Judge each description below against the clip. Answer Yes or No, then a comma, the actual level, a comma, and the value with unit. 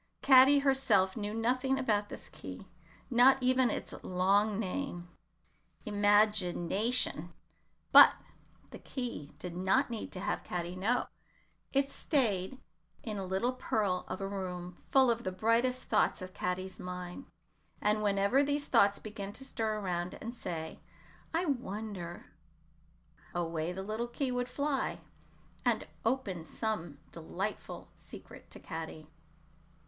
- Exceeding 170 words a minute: No, average, 140 wpm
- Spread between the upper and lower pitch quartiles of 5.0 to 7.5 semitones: Yes, wide, 5.5 semitones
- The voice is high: Yes, high, 210 Hz